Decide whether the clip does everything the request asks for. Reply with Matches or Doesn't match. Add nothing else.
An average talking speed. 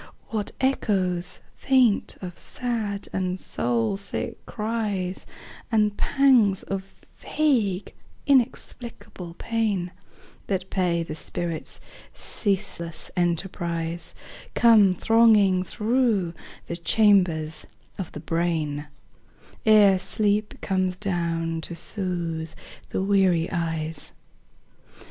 Doesn't match